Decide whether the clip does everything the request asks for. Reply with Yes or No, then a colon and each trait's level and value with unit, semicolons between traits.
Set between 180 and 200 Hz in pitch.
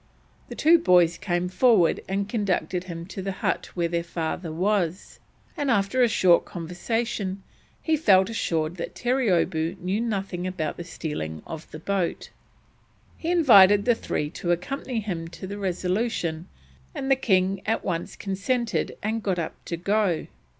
Yes: high, 190 Hz